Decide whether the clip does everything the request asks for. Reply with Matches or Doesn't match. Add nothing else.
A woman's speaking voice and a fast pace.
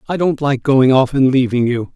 Doesn't match